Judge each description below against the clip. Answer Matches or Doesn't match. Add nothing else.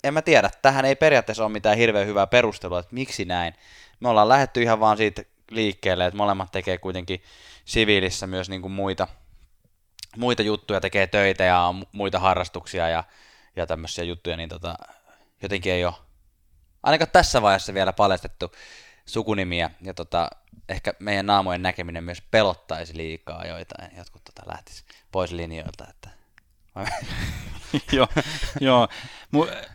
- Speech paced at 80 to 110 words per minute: Doesn't match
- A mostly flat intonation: Doesn't match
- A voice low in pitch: Matches